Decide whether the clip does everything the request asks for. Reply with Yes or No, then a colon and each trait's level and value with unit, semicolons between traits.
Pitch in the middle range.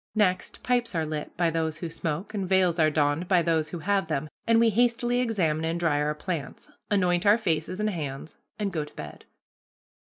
Yes: medium, 170 Hz